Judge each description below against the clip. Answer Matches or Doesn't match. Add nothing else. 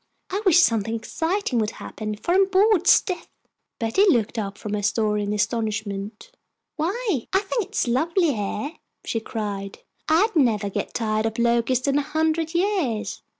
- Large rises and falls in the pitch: Matches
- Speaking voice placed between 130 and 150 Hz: Doesn't match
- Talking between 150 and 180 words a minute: Matches